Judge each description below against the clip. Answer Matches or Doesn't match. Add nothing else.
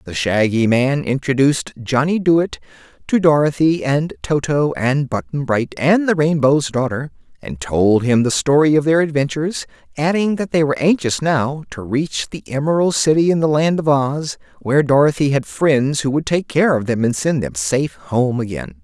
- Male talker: Matches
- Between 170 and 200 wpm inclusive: Matches